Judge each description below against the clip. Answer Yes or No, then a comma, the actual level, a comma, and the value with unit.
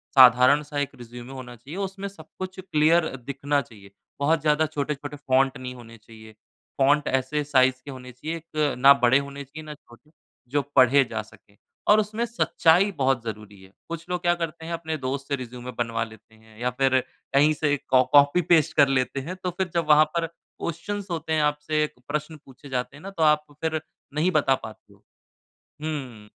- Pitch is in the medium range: Yes, medium, 145 Hz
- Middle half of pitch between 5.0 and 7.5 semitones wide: No, average, 3.9 semitones